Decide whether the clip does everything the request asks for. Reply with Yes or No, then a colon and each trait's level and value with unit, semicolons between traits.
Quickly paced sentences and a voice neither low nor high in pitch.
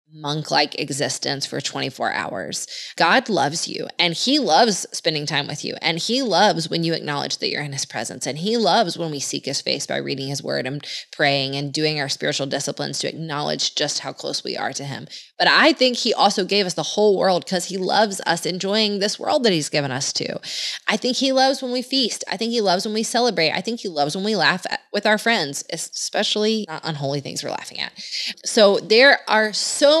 Yes: fast, 225 wpm; medium, 180 Hz